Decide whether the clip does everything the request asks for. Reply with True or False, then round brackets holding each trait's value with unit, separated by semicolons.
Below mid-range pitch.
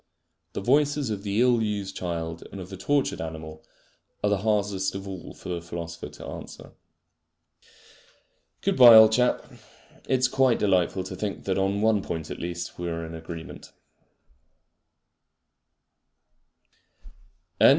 True (95 Hz)